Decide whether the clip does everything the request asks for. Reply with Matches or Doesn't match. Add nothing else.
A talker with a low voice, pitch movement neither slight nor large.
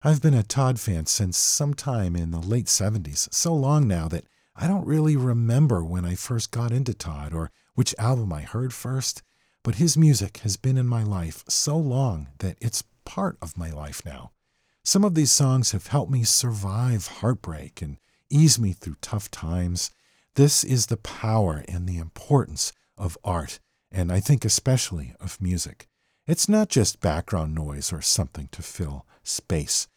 Doesn't match